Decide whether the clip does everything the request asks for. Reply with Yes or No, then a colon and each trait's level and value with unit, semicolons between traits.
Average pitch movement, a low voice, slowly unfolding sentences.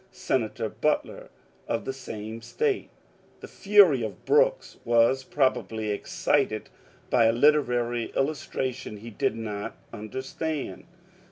Yes: average, 5.0 semitones; low, 125 Hz; slow, 110 wpm